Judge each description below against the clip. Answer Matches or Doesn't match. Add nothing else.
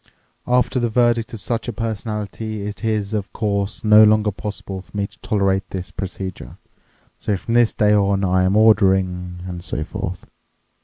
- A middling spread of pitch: Doesn't match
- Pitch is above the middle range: Doesn't match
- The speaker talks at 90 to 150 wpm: Doesn't match